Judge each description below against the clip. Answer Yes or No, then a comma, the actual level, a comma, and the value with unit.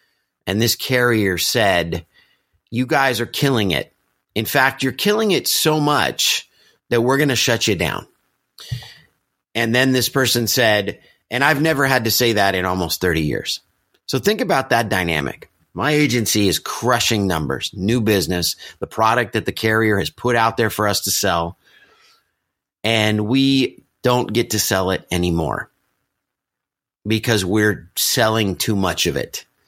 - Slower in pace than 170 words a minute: Yes, average, 160 wpm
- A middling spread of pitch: Yes, average, 4.4 semitones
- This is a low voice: Yes, low, 110 Hz